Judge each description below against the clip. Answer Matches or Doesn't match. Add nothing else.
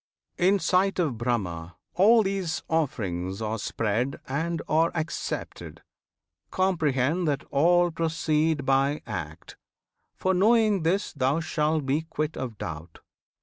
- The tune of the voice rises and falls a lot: Matches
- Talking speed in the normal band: Doesn't match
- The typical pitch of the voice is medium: Matches